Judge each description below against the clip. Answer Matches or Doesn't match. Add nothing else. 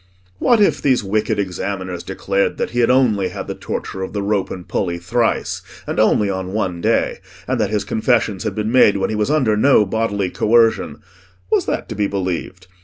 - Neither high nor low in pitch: Doesn't match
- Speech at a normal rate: Matches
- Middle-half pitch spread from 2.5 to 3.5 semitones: Matches